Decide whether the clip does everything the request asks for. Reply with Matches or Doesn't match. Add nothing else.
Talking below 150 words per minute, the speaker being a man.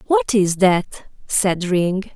Doesn't match